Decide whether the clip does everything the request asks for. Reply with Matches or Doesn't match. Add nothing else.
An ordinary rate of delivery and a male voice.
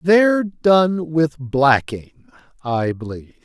Doesn't match